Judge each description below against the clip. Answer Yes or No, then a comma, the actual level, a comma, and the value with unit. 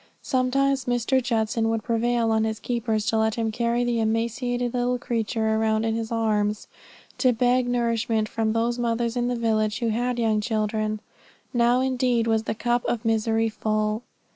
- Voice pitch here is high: Yes, high, 230 Hz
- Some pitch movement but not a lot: No, narrow, 1.7 semitones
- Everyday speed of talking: Yes, average, 170 wpm